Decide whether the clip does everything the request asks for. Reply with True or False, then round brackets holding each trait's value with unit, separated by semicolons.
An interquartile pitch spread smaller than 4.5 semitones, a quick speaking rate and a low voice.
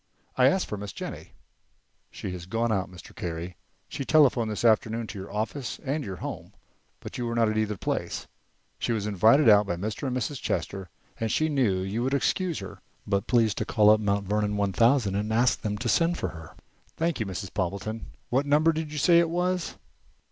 False (5.2 semitones; 215 wpm; 110 Hz)